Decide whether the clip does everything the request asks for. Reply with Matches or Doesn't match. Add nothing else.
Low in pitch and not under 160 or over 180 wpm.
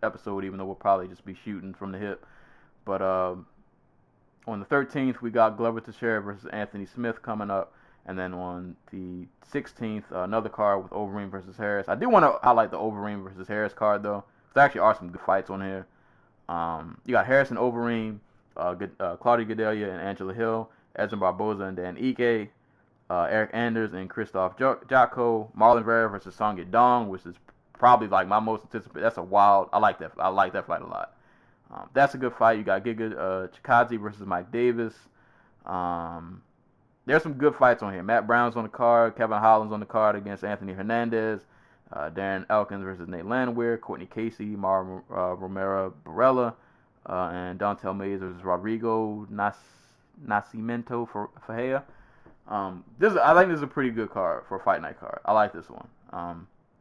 Doesn't match